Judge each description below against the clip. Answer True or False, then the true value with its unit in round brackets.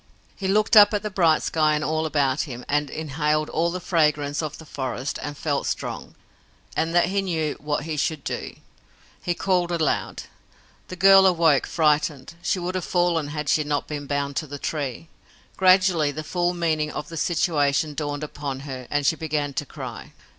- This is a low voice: False (155 Hz)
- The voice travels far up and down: False (3.1 semitones)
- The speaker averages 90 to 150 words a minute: False (190 wpm)